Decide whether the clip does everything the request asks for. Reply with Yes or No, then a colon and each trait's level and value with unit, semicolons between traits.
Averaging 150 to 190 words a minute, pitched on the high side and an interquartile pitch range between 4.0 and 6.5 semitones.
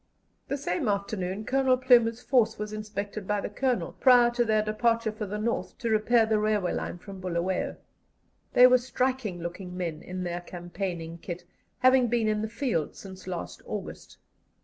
Yes: average, 170 wpm; high, 215 Hz; average, 4.3 semitones